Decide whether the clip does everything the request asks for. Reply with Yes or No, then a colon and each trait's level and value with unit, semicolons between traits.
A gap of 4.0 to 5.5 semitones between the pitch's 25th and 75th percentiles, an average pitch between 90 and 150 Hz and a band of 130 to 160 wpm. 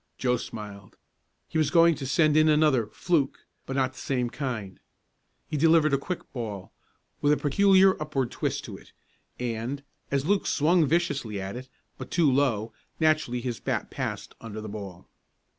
No: average, 5.2 semitones; low, 135 Hz; average, 170 wpm